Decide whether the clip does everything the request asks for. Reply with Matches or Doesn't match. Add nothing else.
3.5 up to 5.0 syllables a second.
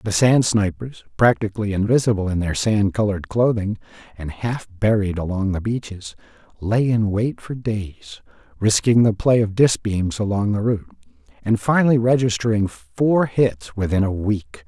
Matches